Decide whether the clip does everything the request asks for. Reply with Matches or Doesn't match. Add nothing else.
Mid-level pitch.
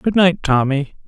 Matches